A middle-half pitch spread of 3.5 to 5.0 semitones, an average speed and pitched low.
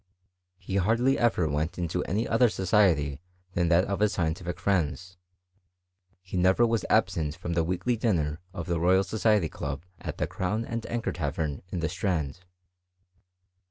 Yes: average, 4.4 semitones; average, 160 wpm; very low, 90 Hz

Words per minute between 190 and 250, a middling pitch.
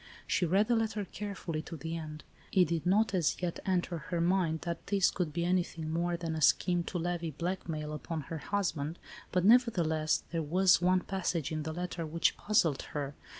Yes: average, 195 wpm; medium, 170 Hz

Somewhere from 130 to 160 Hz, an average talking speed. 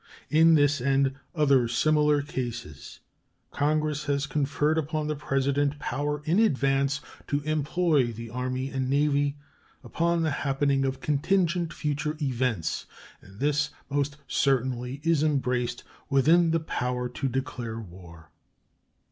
No: medium, 140 Hz; slow, 125 wpm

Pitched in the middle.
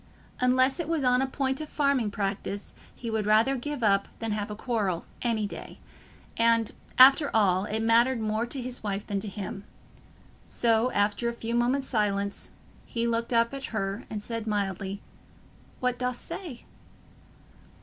No: high, 230 Hz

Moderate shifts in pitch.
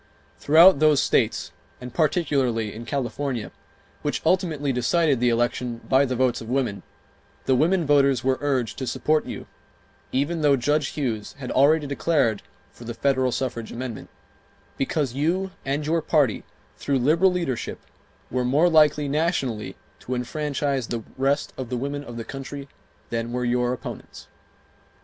Yes: average, 3.4 semitones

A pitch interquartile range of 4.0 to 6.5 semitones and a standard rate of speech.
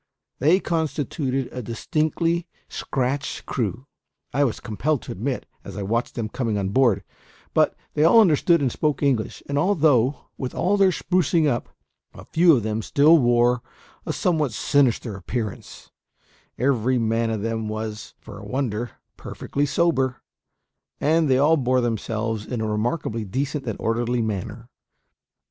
Yes: average, 4.8 semitones; average, 150 wpm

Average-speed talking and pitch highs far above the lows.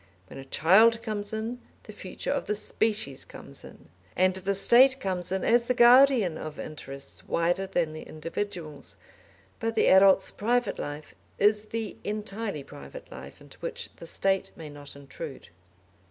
Yes: average, 160 wpm; wide, 6.0 semitones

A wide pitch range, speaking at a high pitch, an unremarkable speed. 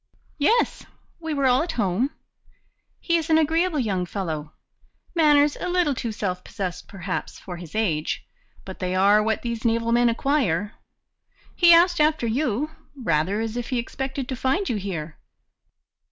Yes: wide, 7.5 semitones; high, 235 Hz; average, 160 wpm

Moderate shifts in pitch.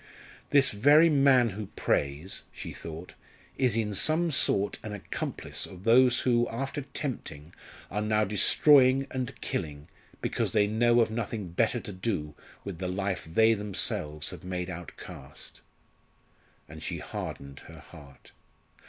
No: wide, 5.7 semitones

